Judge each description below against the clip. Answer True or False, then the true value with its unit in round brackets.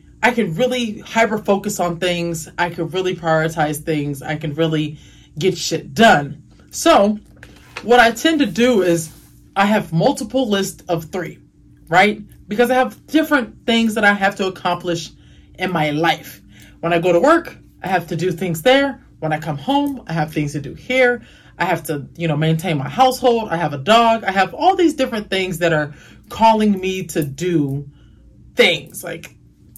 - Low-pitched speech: False (185 Hz)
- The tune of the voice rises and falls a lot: True (6.0 semitones)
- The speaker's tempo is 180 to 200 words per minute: True (185 wpm)